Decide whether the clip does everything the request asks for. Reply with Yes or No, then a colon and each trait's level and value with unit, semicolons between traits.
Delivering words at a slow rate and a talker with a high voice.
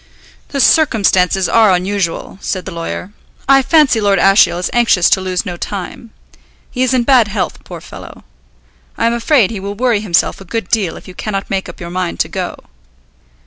No: average, 190 wpm; high, 200 Hz